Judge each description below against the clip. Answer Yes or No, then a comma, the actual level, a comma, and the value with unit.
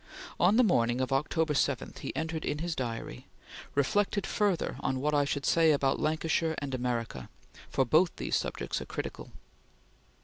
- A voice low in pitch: No, medium, 150 Hz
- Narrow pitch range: No, average, 4.0 semitones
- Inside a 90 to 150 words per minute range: No, average, 165 wpm